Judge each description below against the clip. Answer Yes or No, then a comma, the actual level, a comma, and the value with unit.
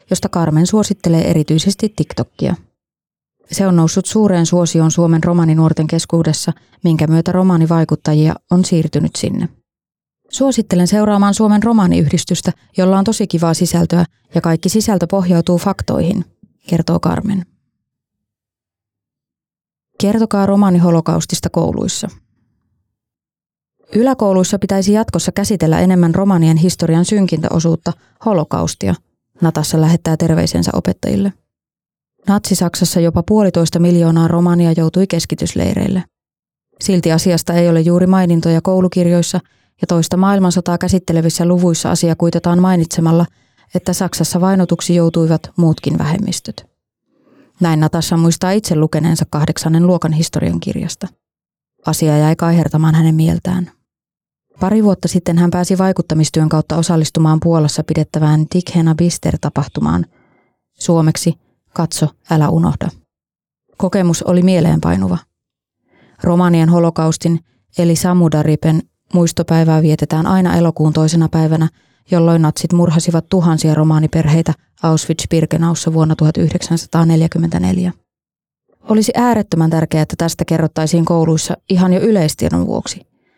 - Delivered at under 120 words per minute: Yes, average, 100 wpm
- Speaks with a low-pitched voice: No, medium, 170 Hz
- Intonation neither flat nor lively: No, narrow, 2.2 semitones